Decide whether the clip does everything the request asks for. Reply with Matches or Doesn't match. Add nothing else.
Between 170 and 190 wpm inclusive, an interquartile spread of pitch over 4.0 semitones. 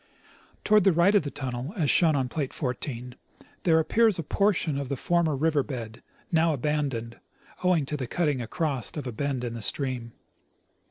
Matches